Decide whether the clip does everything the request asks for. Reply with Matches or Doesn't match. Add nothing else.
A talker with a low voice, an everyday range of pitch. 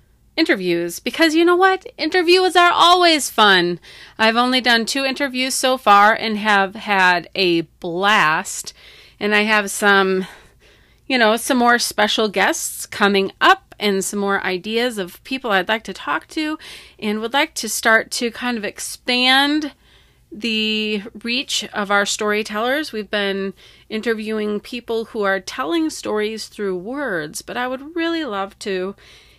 Doesn't match